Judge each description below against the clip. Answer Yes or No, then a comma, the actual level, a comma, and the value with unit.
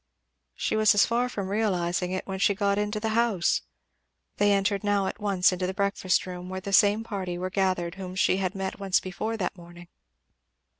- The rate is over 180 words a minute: Yes, average, 200 wpm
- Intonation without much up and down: Yes, narrow, 2.0 semitones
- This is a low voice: No, high, 195 Hz